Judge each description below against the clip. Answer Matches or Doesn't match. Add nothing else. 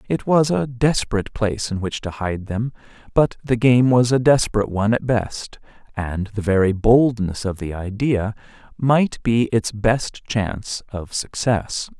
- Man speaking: Matches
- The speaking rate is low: Doesn't match